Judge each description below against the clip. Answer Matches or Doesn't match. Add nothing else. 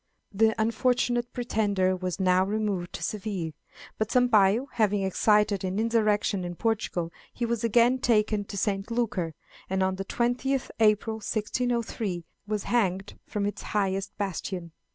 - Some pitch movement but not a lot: Matches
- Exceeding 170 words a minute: Doesn't match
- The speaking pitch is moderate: Doesn't match